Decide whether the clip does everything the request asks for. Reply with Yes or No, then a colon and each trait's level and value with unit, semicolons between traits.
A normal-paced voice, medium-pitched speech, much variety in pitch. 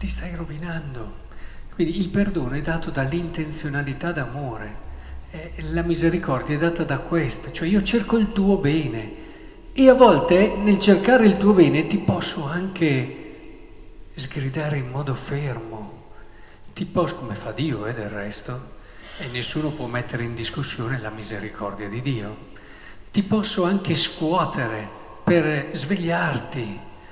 Yes: average, 135 wpm; medium, 150 Hz; wide, 7.1 semitones